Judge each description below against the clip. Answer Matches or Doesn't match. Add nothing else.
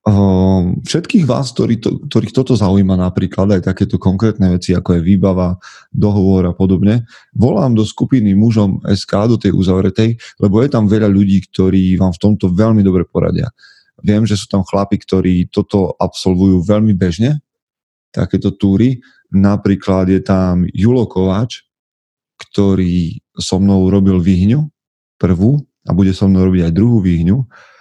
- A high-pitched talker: Doesn't match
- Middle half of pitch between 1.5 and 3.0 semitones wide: Matches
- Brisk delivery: Doesn't match